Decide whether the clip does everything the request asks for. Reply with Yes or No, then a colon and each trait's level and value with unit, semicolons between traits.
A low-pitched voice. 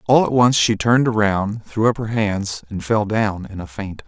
Yes: low, 105 Hz